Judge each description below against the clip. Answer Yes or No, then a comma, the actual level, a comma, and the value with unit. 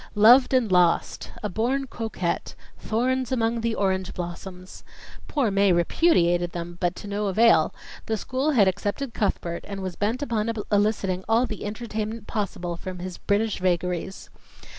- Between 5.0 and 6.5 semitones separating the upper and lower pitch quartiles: No, average, 4.0 semitones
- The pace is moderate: Yes, average, 150 wpm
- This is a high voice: Yes, high, 205 Hz